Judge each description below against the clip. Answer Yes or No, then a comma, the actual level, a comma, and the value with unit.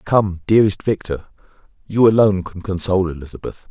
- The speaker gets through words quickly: No, slow, 130 wpm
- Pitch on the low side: Yes, very low, 95 Hz